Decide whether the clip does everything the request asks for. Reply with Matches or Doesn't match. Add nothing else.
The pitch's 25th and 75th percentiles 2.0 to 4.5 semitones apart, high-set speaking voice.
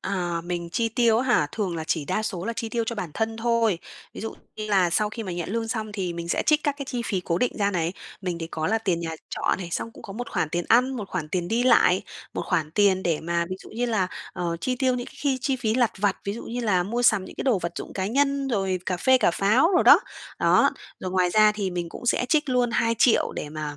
Doesn't match